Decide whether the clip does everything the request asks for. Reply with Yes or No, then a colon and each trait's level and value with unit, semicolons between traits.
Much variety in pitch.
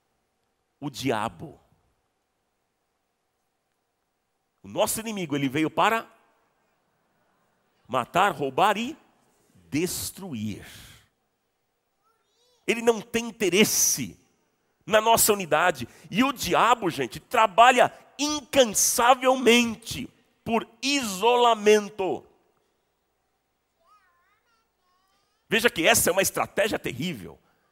Yes: wide, 5.9 semitones